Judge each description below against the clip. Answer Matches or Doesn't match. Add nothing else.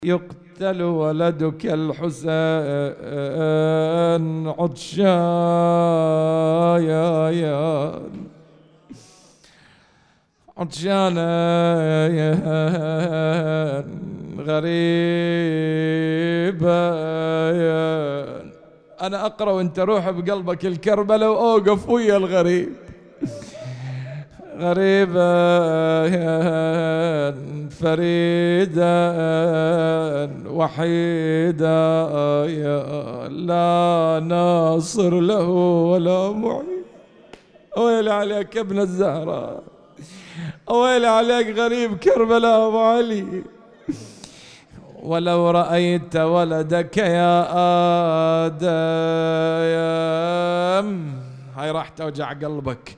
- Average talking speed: Doesn't match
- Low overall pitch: Doesn't match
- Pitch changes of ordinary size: Doesn't match